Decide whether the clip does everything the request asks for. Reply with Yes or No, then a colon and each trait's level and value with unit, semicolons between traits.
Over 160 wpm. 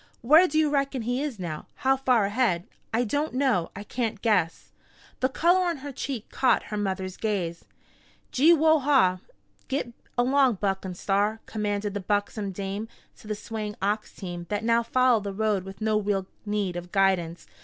Yes: average, 180 wpm